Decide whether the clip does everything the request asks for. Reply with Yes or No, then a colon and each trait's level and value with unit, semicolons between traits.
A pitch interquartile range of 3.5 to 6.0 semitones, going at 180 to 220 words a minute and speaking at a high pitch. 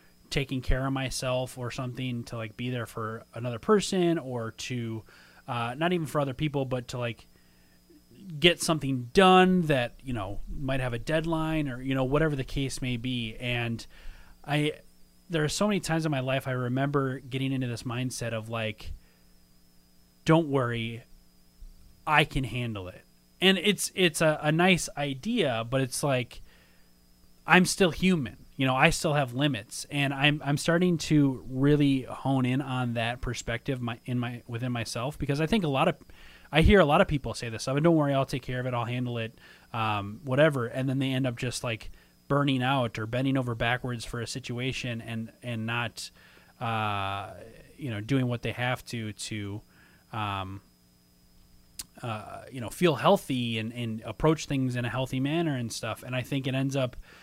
No: average, 4.0 semitones; average, 185 wpm; low, 125 Hz